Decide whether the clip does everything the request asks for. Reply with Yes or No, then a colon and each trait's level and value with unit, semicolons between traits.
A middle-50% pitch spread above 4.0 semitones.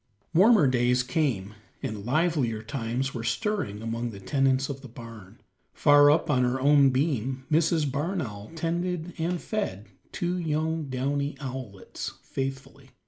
Yes: average, 4.9 semitones